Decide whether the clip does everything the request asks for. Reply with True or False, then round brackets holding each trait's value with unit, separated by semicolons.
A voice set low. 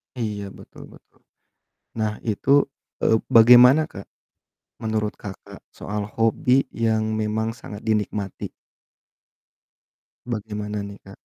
True (110 Hz)